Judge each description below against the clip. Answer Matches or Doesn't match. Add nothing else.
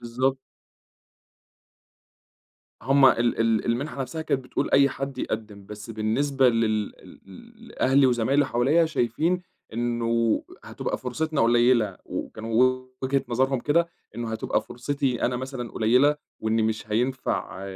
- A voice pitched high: Doesn't match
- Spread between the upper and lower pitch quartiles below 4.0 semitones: Matches